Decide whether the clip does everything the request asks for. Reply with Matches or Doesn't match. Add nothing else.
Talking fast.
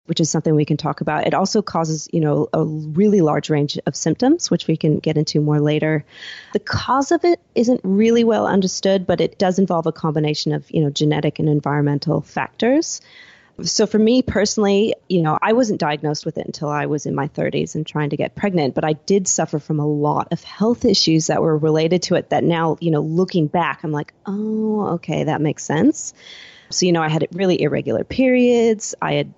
Matches